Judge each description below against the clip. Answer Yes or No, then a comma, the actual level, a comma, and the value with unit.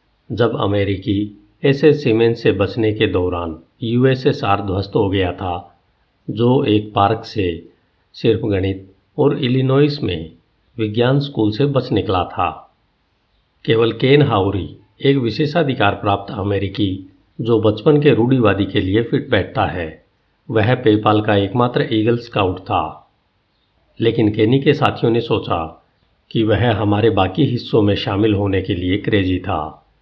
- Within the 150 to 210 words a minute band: No, average, 140 wpm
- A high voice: No, low, 110 Hz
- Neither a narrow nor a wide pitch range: Yes, average, 3.6 semitones